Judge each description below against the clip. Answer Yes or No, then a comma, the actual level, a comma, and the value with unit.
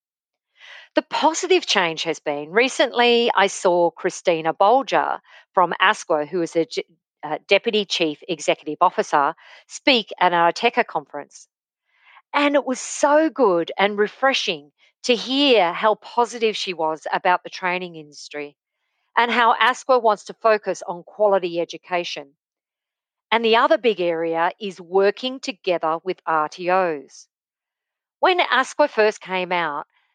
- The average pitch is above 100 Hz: Yes, high, 190 Hz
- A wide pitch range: Yes, wide, 5.7 semitones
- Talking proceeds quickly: No, slow, 135 wpm